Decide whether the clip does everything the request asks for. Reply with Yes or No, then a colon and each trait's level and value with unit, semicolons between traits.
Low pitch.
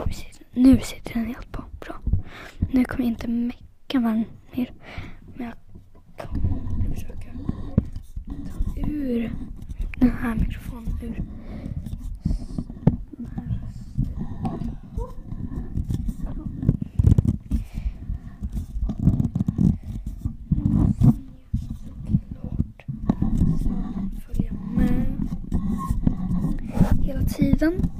No: high, 200 Hz